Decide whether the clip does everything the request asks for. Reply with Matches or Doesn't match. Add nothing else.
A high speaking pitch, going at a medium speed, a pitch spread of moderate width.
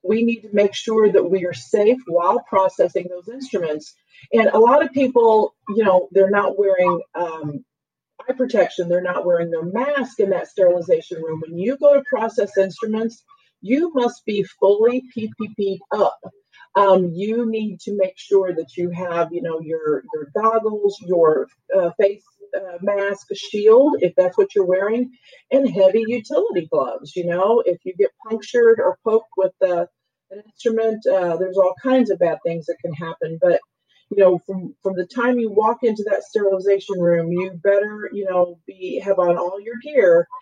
Matches